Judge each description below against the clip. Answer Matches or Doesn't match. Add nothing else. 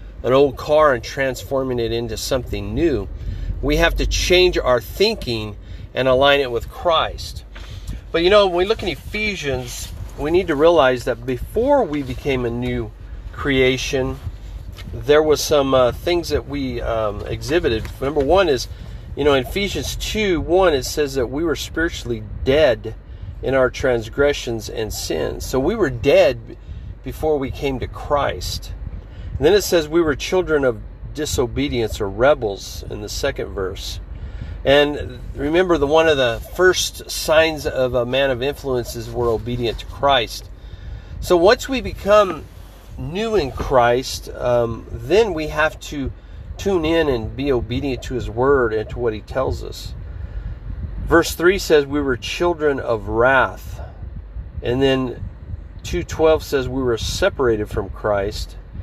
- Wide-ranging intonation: Matches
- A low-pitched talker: Matches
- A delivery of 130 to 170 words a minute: Matches